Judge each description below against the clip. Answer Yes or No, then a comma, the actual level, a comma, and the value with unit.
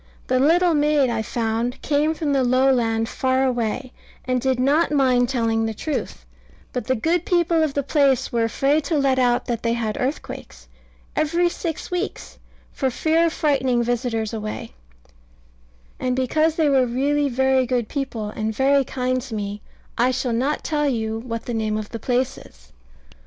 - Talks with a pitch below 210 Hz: No, very high, 255 Hz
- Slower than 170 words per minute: No, average, 175 wpm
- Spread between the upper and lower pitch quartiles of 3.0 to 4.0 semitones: Yes, average, 3.7 semitones